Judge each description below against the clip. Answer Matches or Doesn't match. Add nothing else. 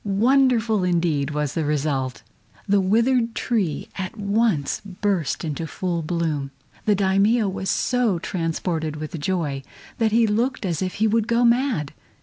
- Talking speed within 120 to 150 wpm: Matches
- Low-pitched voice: Doesn't match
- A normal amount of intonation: Doesn't match